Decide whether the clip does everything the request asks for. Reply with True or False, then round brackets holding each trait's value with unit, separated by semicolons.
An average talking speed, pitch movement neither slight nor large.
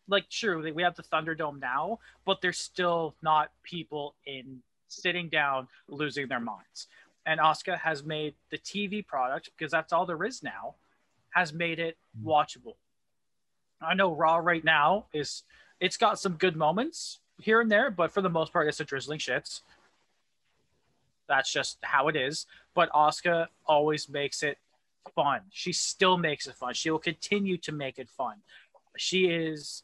True (170 wpm; 3.1 semitones)